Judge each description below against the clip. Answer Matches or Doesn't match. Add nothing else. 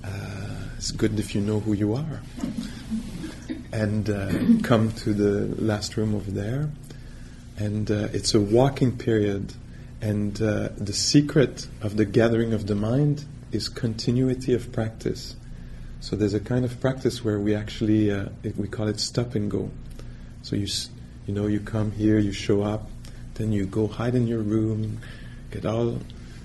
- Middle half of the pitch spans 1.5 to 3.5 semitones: Matches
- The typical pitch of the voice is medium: Doesn't match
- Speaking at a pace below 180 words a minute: Matches